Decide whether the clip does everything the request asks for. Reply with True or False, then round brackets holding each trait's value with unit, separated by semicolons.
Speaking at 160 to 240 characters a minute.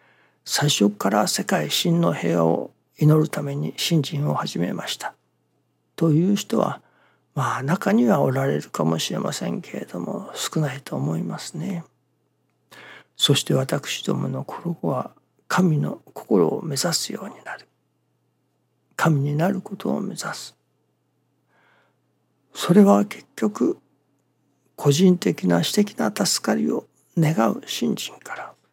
True (230 characters per minute)